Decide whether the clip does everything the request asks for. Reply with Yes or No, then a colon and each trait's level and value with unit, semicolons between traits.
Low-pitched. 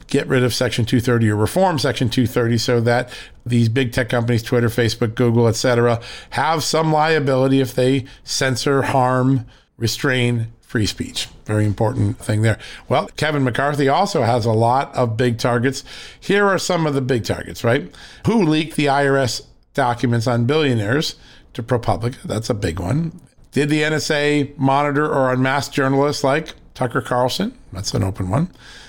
Yes: low, 130 Hz